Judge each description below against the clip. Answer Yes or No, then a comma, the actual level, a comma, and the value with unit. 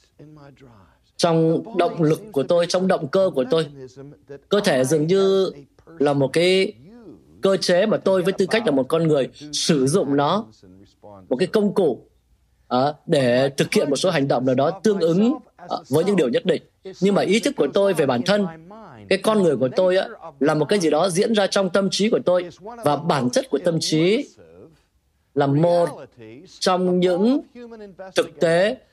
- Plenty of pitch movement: Yes, wide, 5.7 semitones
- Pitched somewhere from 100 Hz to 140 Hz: No, medium, 170 Hz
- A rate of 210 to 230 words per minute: No, average, 190 wpm